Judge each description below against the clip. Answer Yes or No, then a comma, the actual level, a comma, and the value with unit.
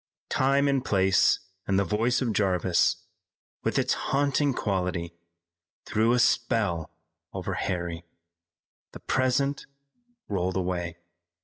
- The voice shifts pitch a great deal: Yes, wide, 5.7 semitones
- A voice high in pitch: No, low, 100 Hz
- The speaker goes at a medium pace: No, slow, 110 wpm